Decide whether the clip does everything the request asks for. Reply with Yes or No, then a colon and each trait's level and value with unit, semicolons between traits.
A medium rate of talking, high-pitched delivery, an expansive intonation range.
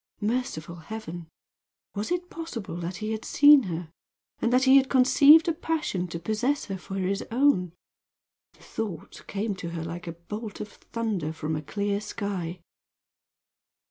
Yes: average, 160 wpm; high, 205 Hz; wide, 6.5 semitones